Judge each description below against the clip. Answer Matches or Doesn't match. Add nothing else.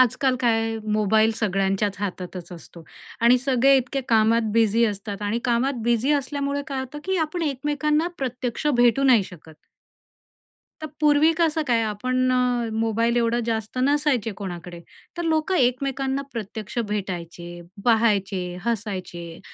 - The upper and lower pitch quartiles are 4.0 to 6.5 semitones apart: Matches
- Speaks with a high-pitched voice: Matches